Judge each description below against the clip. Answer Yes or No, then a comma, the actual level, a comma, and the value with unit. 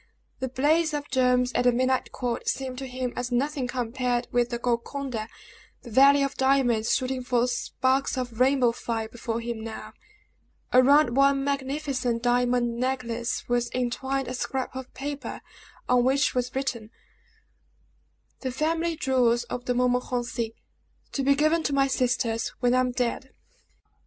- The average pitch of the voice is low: No, very high, 255 Hz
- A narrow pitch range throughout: Yes, narrow, 1.9 semitones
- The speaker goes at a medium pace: Yes, average, 150 wpm